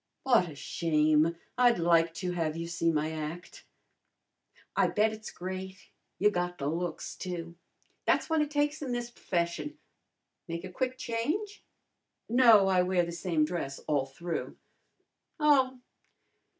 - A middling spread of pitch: No, wide, 6.1 semitones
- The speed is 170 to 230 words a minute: No, average, 145 wpm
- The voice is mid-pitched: Yes, medium, 180 Hz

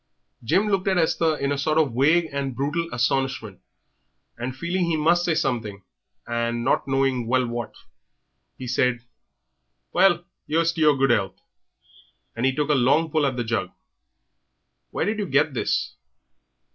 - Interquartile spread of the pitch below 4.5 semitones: No, average, 4.9 semitones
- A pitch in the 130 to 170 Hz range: Yes, medium, 140 Hz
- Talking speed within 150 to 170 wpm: Yes, average, 160 wpm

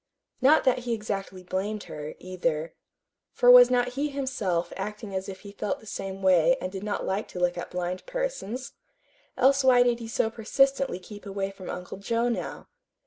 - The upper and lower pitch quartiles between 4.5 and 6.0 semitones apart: Yes, average, 4.8 semitones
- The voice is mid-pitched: No, high, 210 Hz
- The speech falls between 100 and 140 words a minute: No, average, 190 wpm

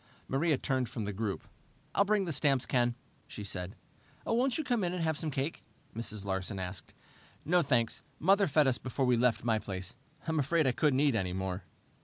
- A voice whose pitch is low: Yes, low, 130 Hz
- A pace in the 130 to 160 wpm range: No, average, 200 wpm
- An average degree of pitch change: No, wide, 7.2 semitones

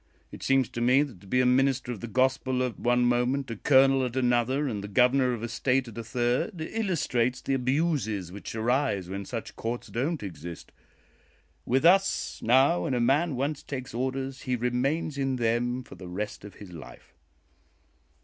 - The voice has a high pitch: No, low, 125 Hz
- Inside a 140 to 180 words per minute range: No, average, 190 wpm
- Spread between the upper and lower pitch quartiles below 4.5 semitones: Yes, narrow, 2.5 semitones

